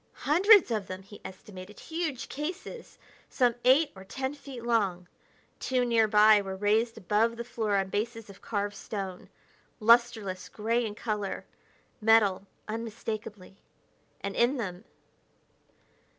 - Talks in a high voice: Yes, high, 220 Hz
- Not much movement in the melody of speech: No, average, 3.2 semitones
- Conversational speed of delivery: No, slow, 125 wpm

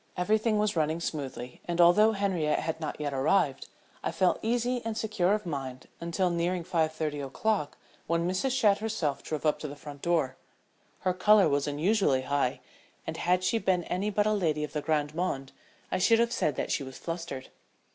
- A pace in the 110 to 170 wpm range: No, average, 195 wpm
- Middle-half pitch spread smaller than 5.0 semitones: No, wide, 5.5 semitones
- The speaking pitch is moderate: Yes, medium, 170 Hz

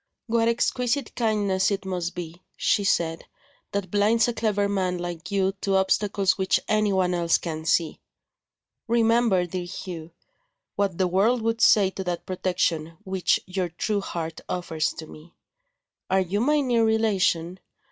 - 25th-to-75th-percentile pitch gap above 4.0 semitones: No, average, 3.4 semitones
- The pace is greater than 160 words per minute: No, average, 150 wpm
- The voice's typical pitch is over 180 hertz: Yes, high, 190 Hz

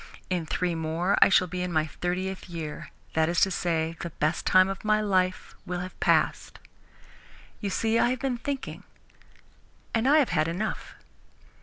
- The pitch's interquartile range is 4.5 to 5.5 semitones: No, average, 3.7 semitones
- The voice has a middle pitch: Yes, medium, 180 Hz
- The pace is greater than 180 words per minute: No, average, 175 wpm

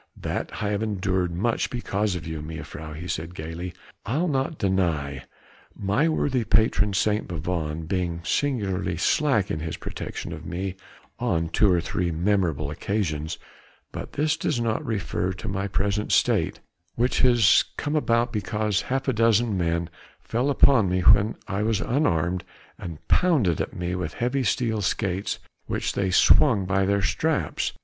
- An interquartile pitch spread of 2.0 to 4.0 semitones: No, average, 4.9 semitones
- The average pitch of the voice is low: Yes, low, 100 Hz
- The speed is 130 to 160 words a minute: Yes, average, 155 wpm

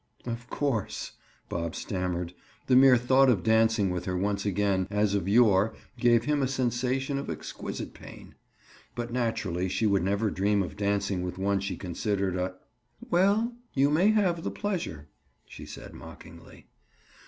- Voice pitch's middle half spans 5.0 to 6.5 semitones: Yes, wide, 5.4 semitones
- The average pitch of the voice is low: Yes, low, 105 Hz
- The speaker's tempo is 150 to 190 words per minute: Yes, average, 155 wpm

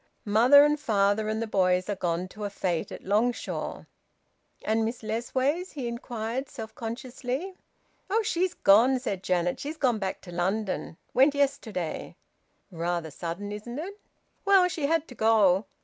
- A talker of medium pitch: No, high, 225 Hz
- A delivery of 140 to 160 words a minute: Yes, average, 155 wpm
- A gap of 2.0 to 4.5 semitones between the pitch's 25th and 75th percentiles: No, wide, 5.6 semitones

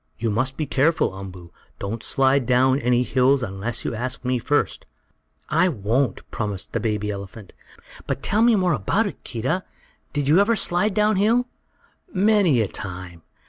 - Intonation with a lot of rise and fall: Yes, wide, 8.6 semitones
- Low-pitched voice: Yes, low, 130 Hz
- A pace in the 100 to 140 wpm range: No, average, 165 wpm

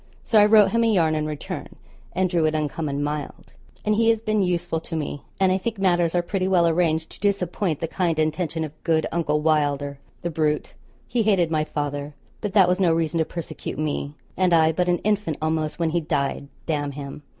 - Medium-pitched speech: Yes, medium, 165 Hz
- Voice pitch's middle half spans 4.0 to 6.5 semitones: No, average, 3.3 semitones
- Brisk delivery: Yes, fast, 215 wpm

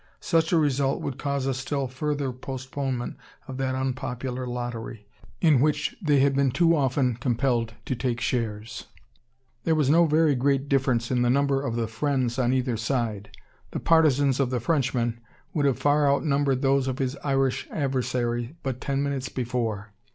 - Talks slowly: No, average, 170 wpm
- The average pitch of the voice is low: Yes, low, 130 Hz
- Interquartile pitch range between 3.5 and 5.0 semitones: No, narrow, 2.5 semitones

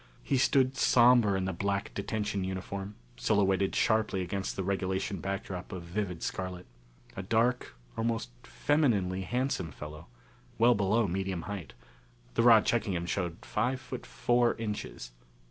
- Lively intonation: No, average, 3.7 semitones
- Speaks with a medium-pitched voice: No, low, 100 Hz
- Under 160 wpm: Yes, average, 140 wpm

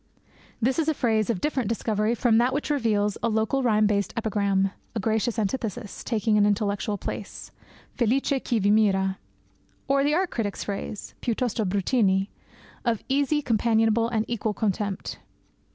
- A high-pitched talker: Yes, high, 220 Hz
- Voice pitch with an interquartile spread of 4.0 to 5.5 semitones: No, average, 2.9 semitones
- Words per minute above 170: No, average, 150 wpm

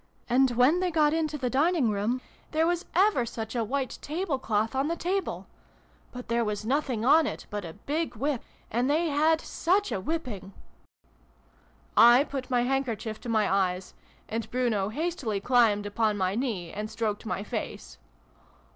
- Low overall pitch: No, high, 245 Hz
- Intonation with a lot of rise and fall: Yes, wide, 5.9 semitones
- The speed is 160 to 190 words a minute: Yes, average, 175 wpm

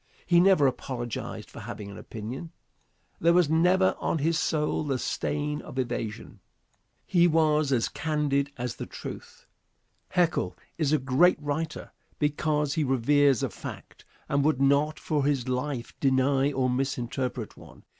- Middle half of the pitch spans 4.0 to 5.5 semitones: No, average, 3.1 semitones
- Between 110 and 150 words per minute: Yes, average, 145 wpm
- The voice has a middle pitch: Yes, medium, 145 Hz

